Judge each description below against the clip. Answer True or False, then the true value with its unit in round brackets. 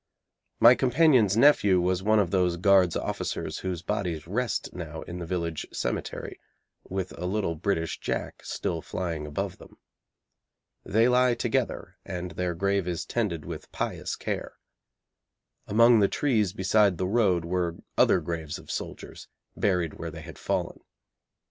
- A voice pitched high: False (95 Hz)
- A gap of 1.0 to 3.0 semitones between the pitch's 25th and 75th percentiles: False (3.7 semitones)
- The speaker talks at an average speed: True (150 wpm)